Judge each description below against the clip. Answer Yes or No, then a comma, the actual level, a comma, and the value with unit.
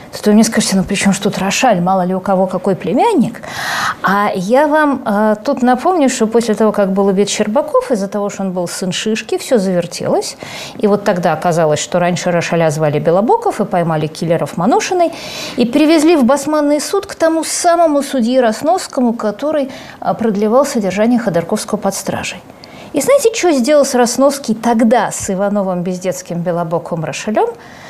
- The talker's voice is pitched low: No, high, 215 Hz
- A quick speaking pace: Yes, fast, 165 wpm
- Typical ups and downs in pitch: No, wide, 6.6 semitones